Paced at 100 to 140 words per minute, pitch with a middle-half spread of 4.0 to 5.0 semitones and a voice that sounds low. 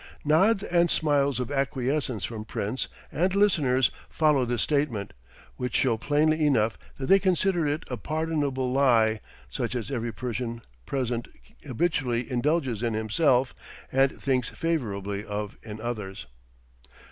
Yes: slow, 135 wpm; average, 4.6 semitones; low, 130 Hz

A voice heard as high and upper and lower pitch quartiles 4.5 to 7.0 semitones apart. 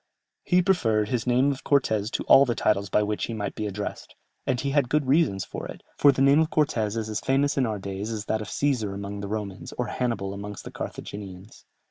No: low, 110 Hz; average, 5.0 semitones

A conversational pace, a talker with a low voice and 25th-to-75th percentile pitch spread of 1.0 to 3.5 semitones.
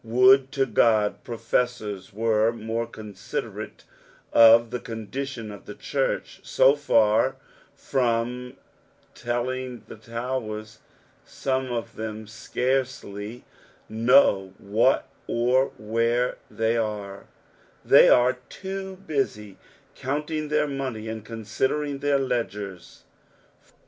No: slow, 100 wpm; low, 115 Hz; average, 3.2 semitones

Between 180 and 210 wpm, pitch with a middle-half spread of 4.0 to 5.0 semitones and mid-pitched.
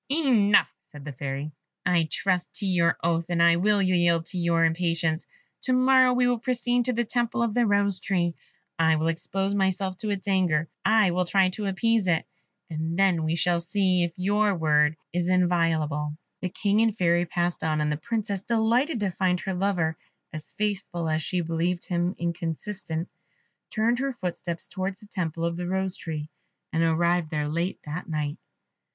No: average, 185 wpm; average, 3.5 semitones; medium, 180 Hz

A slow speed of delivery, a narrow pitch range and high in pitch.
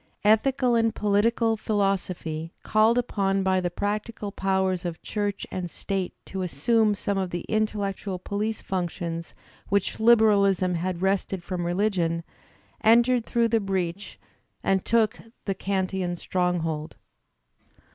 No: slow, 125 wpm; average, 3.1 semitones; high, 195 Hz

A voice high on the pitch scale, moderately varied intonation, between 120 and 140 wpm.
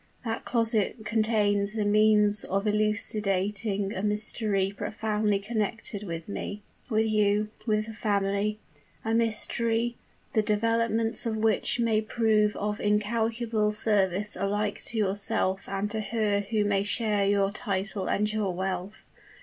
No: high, 210 Hz; narrow, 1.5 semitones; slow, 135 wpm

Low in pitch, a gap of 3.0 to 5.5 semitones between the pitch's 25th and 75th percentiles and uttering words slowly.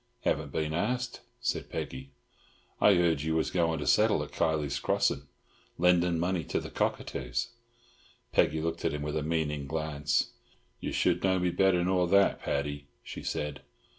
No: very low, 80 Hz; average, 3.3 semitones; average, 165 wpm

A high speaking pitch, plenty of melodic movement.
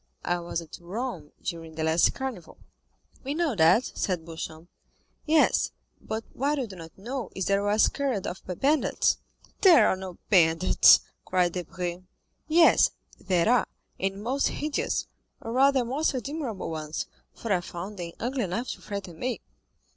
Yes: high, 195 Hz; wide, 6.9 semitones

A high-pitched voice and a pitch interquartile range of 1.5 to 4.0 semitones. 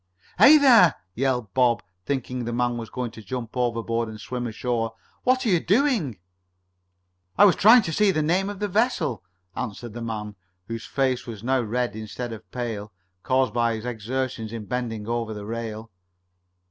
No: low, 120 Hz; average, 3.3 semitones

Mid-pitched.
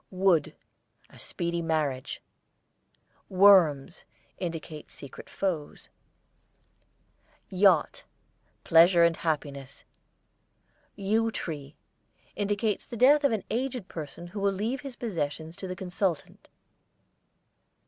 Yes: medium, 180 Hz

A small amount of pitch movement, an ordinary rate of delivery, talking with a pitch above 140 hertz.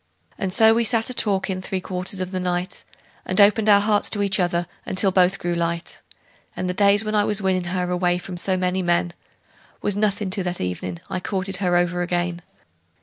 No: narrow, 2.3 semitones; fast, 210 wpm; medium, 185 Hz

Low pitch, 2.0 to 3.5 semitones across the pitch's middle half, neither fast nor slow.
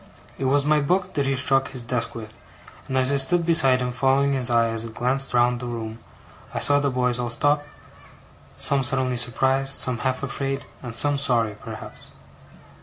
Yes: low, 130 Hz; narrow, 2.4 semitones; average, 190 wpm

